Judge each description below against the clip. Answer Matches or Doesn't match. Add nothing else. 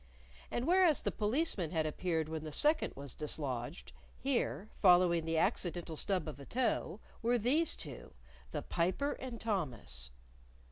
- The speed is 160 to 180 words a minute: Doesn't match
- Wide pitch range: Matches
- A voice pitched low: Doesn't match